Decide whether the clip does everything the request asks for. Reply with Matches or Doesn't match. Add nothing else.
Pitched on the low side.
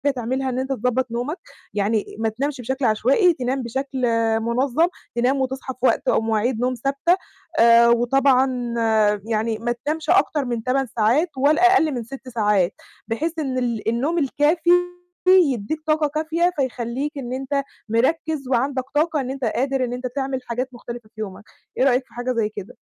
Doesn't match